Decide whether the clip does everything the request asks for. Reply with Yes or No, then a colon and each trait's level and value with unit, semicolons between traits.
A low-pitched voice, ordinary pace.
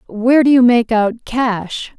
No: high, 235 Hz; average, 180 wpm